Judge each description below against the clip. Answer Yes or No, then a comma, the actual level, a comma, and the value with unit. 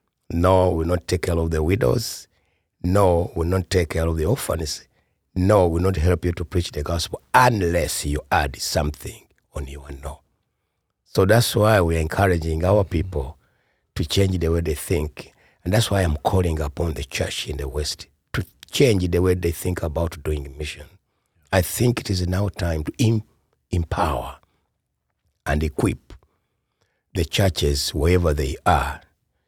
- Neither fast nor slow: Yes, average, 175 wpm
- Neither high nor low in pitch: No, very low, 85 Hz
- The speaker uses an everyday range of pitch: Yes, average, 3.6 semitones